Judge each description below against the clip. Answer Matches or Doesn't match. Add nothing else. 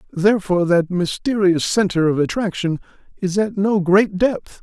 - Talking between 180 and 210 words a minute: Doesn't match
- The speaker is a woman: Doesn't match